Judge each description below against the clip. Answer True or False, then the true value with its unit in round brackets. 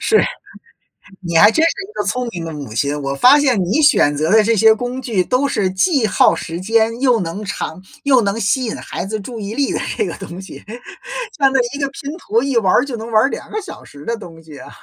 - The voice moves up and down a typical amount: False (6.2 semitones)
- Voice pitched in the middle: False (220 Hz)